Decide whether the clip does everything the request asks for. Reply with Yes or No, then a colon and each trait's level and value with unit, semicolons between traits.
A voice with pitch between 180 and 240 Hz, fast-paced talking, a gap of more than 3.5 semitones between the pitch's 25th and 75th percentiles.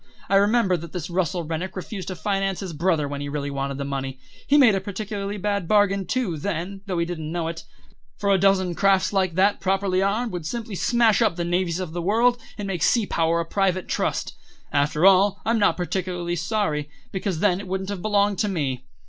No: medium, 185 Hz; fast, 215 wpm; average, 3.2 semitones